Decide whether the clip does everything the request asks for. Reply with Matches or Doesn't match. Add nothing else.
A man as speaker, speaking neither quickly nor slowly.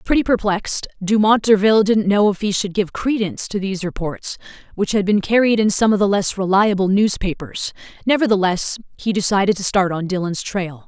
Doesn't match